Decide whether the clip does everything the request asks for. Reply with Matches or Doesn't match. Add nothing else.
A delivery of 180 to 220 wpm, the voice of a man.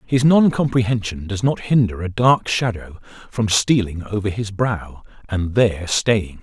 Doesn't match